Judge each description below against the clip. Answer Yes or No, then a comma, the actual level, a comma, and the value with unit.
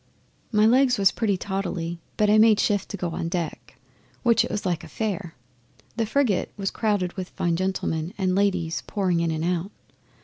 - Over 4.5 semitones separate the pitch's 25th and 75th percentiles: No, average, 3.4 semitones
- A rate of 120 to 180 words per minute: No, average, 190 wpm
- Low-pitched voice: No, high, 190 Hz